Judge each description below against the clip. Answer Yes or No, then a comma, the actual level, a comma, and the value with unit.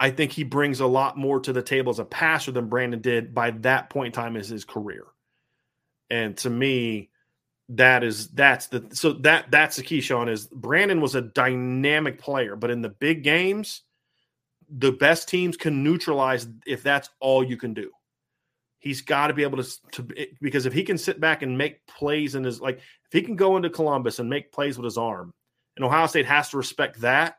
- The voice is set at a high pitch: No, low, 135 Hz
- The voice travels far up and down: No, average, 2.9 semitones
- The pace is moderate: No, fast, 215 wpm